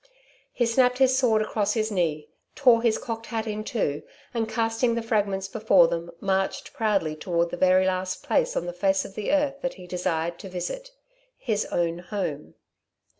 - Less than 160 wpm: No, average, 180 wpm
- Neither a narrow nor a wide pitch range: Yes, average, 4.3 semitones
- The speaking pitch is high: Yes, high, 205 Hz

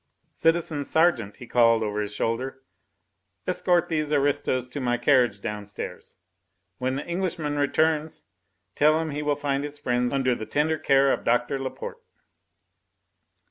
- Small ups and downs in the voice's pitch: No, average, 4.0 semitones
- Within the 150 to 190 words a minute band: No, average, 140 wpm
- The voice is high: No, medium, 140 Hz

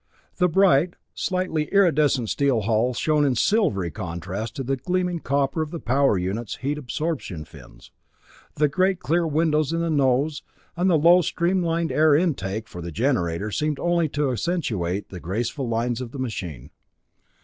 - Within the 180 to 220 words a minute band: No, average, 160 wpm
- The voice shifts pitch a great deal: Yes, wide, 7.0 semitones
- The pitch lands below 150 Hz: Yes, medium, 140 Hz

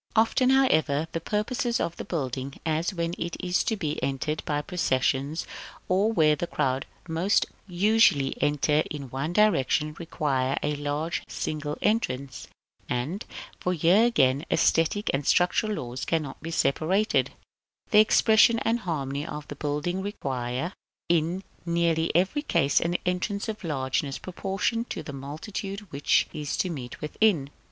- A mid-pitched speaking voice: Yes, medium, 160 Hz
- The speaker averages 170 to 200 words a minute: No, average, 145 wpm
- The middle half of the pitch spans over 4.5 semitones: Yes, average, 5.2 semitones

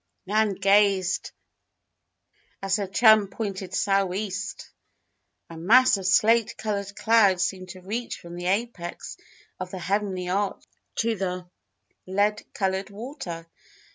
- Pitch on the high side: Yes, high, 195 Hz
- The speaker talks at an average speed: No, slow, 120 wpm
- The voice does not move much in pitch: Yes, narrow, 2.3 semitones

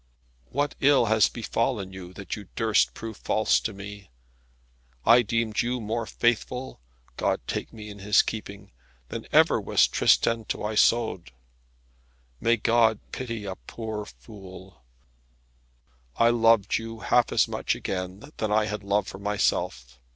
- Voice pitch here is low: Yes, low, 110 Hz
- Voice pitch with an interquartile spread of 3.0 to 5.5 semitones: No, narrow, 2.6 semitones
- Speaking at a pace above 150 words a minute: No, average, 145 wpm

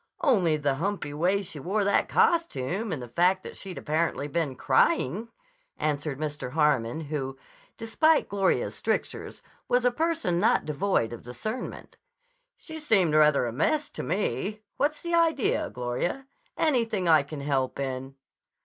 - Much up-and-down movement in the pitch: Yes, wide, 7.6 semitones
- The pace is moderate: Yes, average, 150 wpm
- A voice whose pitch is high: No, medium, 170 Hz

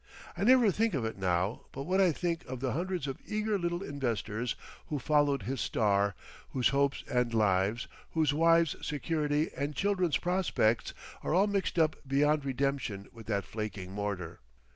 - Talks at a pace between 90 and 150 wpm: No, average, 165 wpm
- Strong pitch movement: Yes, wide, 7.0 semitones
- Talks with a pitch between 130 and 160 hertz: Yes, medium, 140 Hz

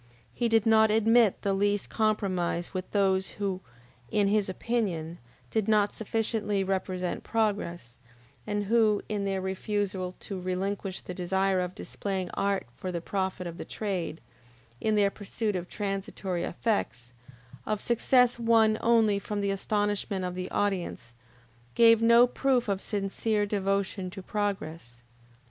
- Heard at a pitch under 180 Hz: No, high, 200 Hz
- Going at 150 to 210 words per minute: No, average, 140 wpm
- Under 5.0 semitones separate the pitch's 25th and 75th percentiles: Yes, narrow, 2.6 semitones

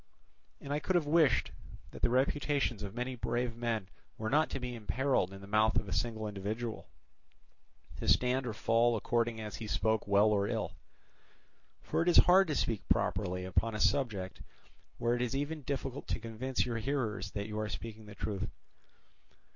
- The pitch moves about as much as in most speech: Yes, average, 3.6 semitones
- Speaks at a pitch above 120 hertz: No, low, 115 Hz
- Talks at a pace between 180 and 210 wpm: Yes, average, 185 wpm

